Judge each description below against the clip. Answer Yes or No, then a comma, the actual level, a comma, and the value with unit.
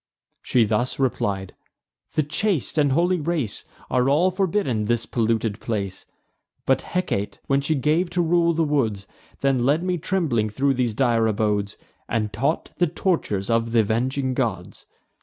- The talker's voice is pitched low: Yes, low, 130 Hz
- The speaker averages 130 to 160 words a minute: Yes, average, 155 wpm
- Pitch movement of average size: No, wide, 6.5 semitones